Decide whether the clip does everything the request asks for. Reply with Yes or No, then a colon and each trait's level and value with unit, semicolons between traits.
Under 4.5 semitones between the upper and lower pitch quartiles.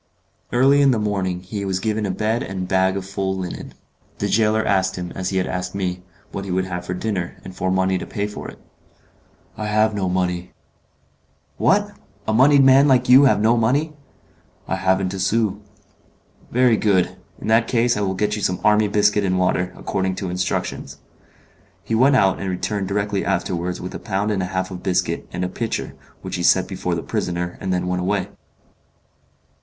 Yes: average, 2.8 semitones